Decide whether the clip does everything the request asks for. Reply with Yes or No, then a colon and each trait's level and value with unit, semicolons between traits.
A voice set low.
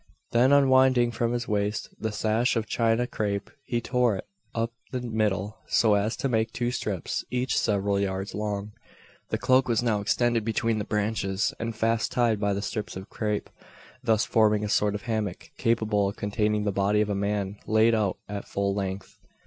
Yes: low, 110 Hz